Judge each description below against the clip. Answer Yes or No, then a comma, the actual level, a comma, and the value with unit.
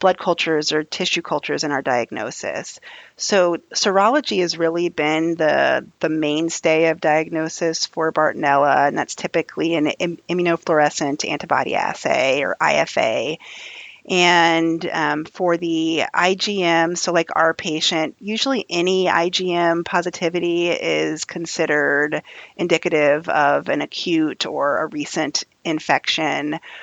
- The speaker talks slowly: Yes, slow, 120 wpm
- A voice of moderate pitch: Yes, medium, 165 Hz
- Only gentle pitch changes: Yes, narrow, 2.2 semitones